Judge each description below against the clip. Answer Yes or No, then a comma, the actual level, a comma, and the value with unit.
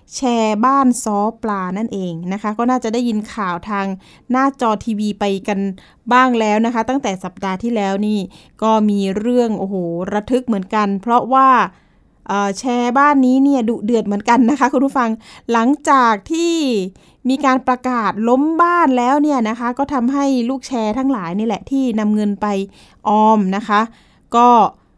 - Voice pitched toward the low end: No, high, 225 Hz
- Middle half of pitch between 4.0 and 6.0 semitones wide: No, average, 3.6 semitones